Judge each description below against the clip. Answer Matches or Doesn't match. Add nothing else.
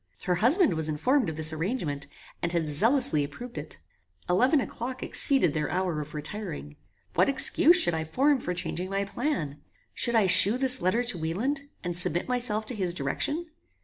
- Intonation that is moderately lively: Doesn't match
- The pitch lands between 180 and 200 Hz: Matches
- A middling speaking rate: Matches